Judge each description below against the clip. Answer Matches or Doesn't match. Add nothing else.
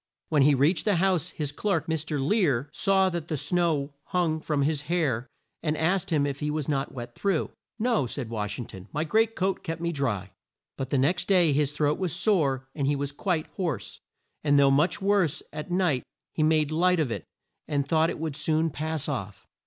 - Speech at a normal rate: Doesn't match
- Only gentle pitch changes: Doesn't match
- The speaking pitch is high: Doesn't match